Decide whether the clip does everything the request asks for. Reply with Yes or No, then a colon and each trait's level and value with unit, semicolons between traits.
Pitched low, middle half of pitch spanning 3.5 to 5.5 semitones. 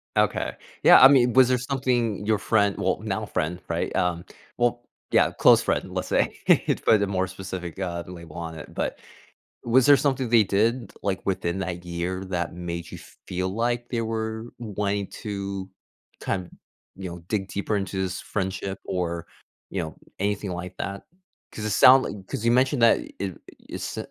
Yes: low, 100 Hz; average, 4.1 semitones